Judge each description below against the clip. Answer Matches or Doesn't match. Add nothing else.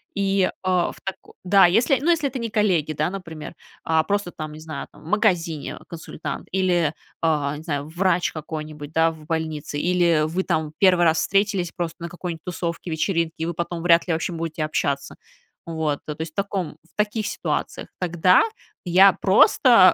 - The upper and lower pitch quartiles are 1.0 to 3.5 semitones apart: Matches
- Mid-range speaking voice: Matches